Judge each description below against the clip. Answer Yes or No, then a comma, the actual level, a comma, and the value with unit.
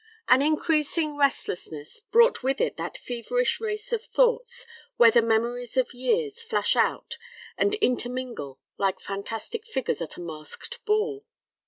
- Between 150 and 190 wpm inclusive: No, average, 140 wpm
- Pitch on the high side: Yes, very high, 285 Hz